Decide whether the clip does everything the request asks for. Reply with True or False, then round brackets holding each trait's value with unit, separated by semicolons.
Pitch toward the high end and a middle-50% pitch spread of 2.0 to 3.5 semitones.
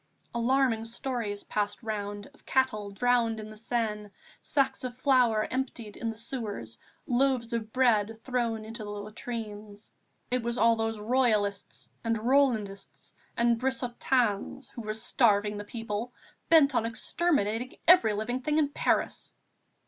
True (230 Hz; 3.0 semitones)